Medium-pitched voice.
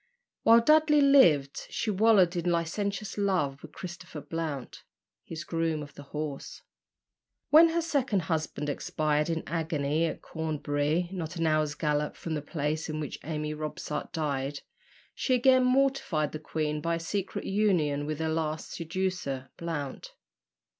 Yes: medium, 160 Hz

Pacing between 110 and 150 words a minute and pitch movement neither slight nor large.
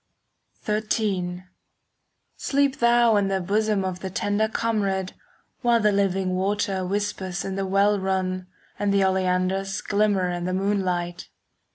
No: average, 140 wpm; narrow, 1.9 semitones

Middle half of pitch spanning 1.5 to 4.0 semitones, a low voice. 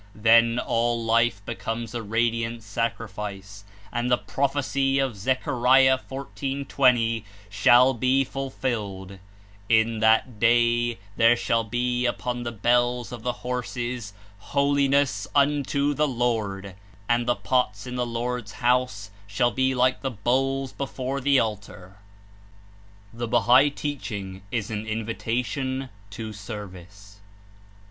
Yes: average, 2.8 semitones; low, 120 Hz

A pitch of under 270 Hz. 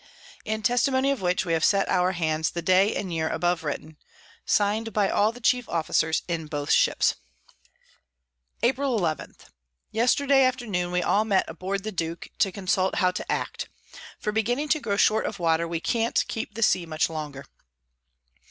Yes: high, 190 Hz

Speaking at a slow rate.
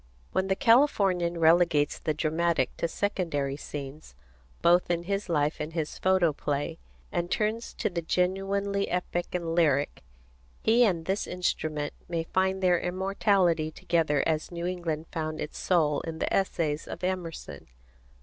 No: average, 145 wpm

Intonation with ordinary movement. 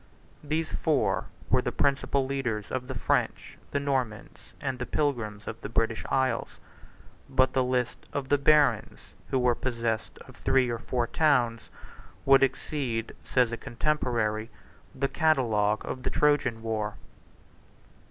Yes: average, 3.3 semitones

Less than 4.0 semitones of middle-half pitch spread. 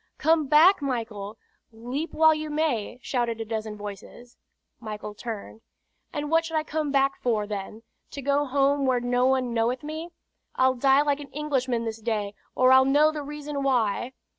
No: average, 4.4 semitones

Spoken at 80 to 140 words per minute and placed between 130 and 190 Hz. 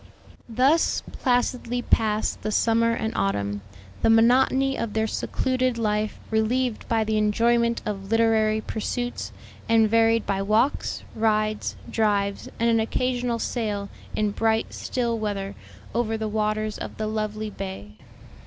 No: slow, 135 wpm; high, 220 Hz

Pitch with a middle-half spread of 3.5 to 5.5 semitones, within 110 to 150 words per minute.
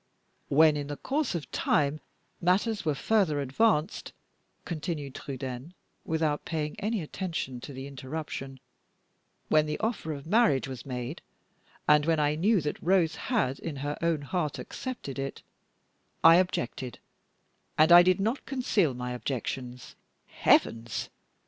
Yes: average, 4.7 semitones; average, 140 wpm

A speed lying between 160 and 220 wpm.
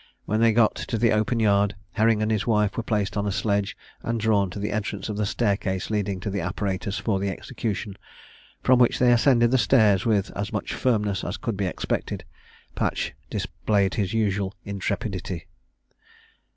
Yes: average, 185 wpm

